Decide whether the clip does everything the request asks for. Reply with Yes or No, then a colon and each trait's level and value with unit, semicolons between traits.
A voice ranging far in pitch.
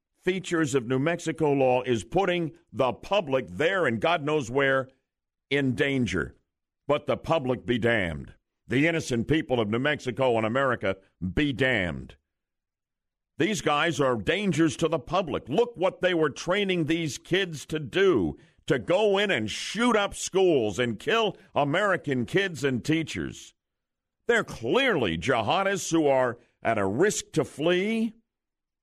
Yes: wide, 6.0 semitones